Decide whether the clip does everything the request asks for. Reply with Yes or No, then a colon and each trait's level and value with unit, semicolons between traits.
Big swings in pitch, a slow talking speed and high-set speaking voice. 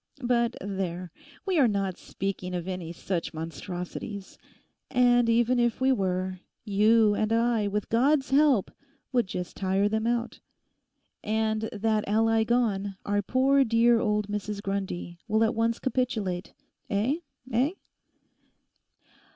No: average, 3.5 semitones; slow, 125 wpm; high, 215 Hz